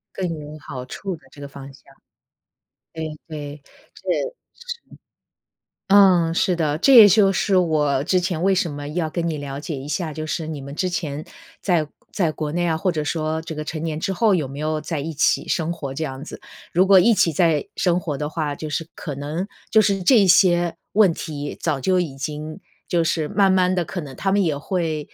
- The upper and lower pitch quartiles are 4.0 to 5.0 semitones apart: No, average, 3.5 semitones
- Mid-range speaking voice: Yes, medium, 160 Hz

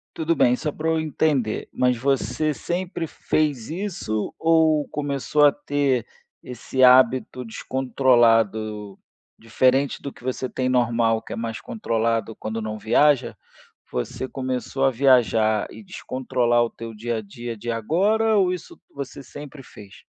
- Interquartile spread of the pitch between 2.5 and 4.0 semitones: No, average, 4.5 semitones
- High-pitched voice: No, low, 130 Hz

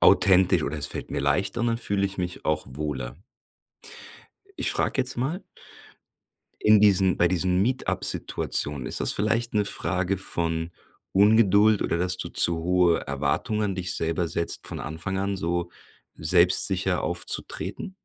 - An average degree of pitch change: Yes, average, 3.5 semitones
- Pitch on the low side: Yes, very low, 90 Hz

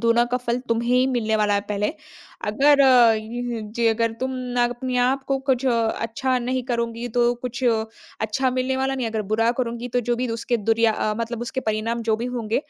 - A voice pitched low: No, high, 240 Hz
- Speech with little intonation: Yes, narrow, 1.9 semitones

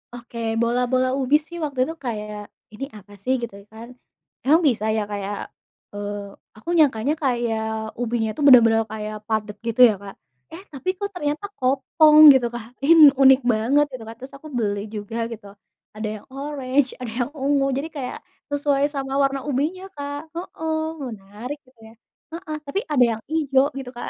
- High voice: Yes, very high, 255 Hz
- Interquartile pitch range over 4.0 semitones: Yes, average, 4.6 semitones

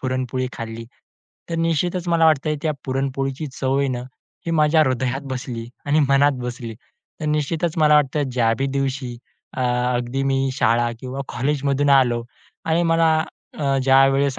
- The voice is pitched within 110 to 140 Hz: Yes, low, 135 Hz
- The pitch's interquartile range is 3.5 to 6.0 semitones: No, average, 2.8 semitones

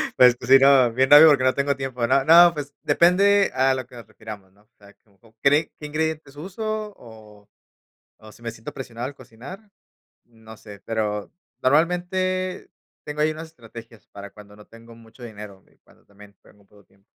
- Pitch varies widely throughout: Yes, wide, 5.9 semitones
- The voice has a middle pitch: No, low, 130 Hz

